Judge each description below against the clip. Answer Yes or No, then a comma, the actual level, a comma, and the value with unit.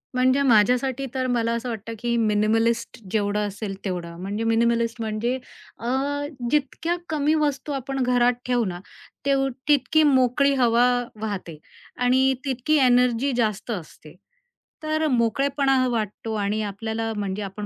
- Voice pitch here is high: Yes, high, 235 Hz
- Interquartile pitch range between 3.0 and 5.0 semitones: Yes, average, 3.7 semitones